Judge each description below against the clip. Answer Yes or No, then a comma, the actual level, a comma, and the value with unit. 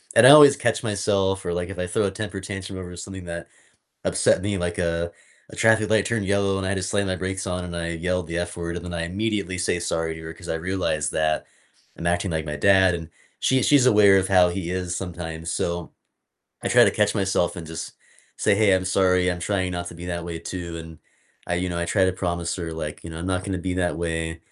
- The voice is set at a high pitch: No, very low, 90 Hz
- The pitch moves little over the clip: Yes, narrow, 2.2 semitones